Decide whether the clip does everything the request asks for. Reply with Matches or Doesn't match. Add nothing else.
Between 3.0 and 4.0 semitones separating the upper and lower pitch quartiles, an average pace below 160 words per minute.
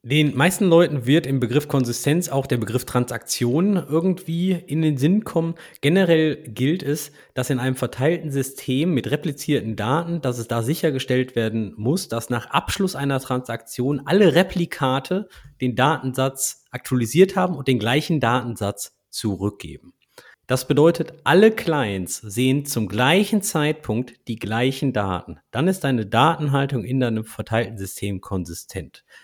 Doesn't match